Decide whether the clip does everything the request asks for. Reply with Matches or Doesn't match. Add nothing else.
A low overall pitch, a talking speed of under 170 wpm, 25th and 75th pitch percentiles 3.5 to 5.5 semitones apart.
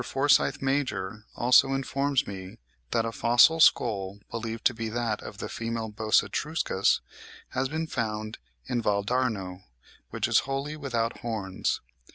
Matches